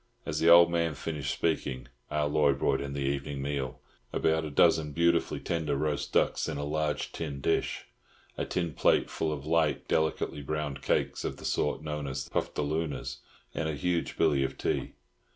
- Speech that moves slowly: No, average, 175 wpm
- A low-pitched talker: Yes, very low, 75 Hz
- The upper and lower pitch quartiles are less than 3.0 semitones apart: Yes, narrow, 2.4 semitones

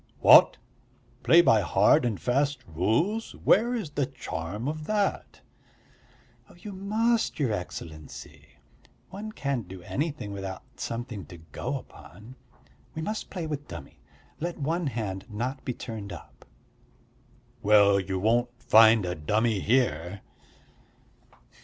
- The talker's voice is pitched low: Yes, low, 115 Hz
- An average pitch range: No, wide, 7.9 semitones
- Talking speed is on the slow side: Yes, slow, 125 wpm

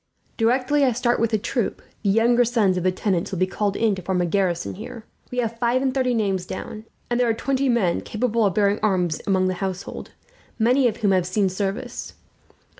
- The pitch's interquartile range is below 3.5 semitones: No, average, 4.3 semitones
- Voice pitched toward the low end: No, high, 215 Hz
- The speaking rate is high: Yes, fast, 215 wpm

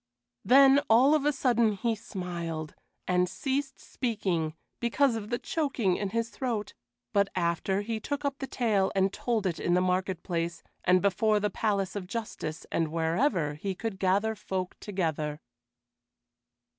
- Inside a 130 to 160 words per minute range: Yes, average, 155 wpm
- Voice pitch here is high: Yes, high, 200 Hz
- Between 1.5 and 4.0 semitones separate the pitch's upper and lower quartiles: No, average, 4.6 semitones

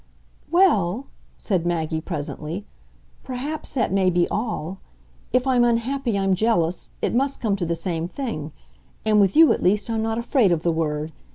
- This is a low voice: No, high, 200 Hz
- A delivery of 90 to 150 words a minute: No, average, 170 wpm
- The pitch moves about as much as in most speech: No, wide, 5.9 semitones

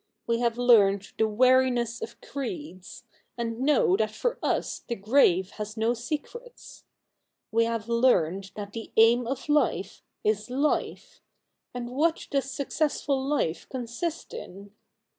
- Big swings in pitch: No, average, 4.1 semitones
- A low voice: No, high, 235 Hz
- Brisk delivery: No, slow, 135 wpm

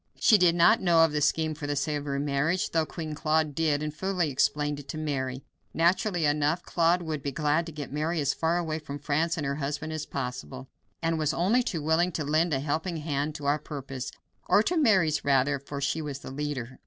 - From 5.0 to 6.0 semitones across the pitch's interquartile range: No, narrow, 2.4 semitones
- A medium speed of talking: No, fast, 215 wpm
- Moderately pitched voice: Yes, medium, 150 Hz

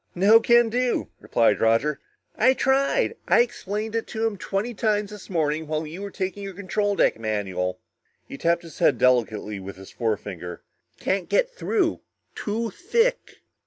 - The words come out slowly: No, average, 160 wpm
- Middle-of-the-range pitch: No, high, 195 Hz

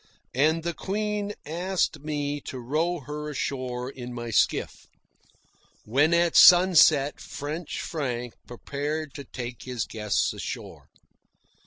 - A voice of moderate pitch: Yes, medium, 145 Hz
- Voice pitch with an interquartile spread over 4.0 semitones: Yes, average, 4.8 semitones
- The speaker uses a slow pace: Yes, slow, 120 wpm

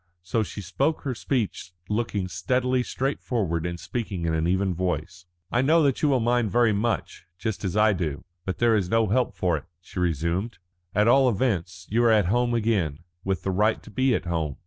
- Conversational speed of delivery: No, fast, 210 wpm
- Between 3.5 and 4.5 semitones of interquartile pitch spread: No, average, 5.2 semitones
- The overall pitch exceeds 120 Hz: No, low, 105 Hz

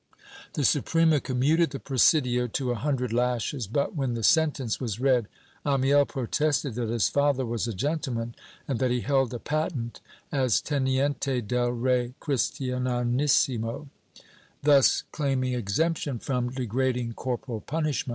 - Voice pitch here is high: No, low, 130 Hz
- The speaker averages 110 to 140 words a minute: Yes, slow, 135 wpm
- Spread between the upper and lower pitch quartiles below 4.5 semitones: Yes, average, 2.8 semitones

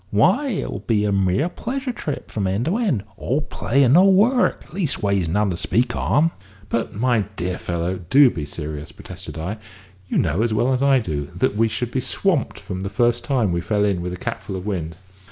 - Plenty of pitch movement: Yes, wide, 7.1 semitones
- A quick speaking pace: Yes, fast, 210 wpm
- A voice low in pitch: Yes, low, 105 Hz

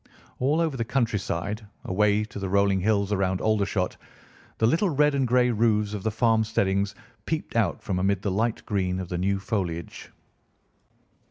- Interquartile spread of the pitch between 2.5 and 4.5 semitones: Yes, average, 2.9 semitones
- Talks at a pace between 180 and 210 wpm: No, average, 170 wpm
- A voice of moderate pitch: No, low, 105 Hz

